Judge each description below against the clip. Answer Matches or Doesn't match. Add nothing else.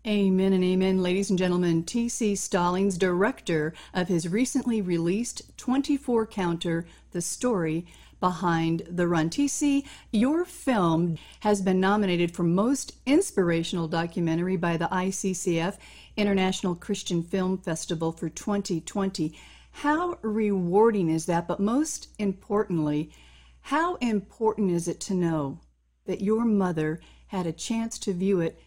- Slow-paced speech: Matches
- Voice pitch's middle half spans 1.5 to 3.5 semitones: Doesn't match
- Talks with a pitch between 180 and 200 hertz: Matches